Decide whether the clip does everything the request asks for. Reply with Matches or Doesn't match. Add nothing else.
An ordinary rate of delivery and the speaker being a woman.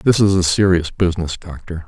Doesn't match